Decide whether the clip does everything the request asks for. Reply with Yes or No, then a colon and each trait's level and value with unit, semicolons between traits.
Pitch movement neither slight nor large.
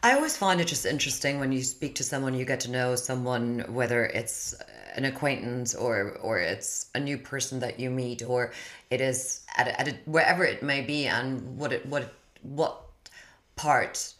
No: narrow, 2.1 semitones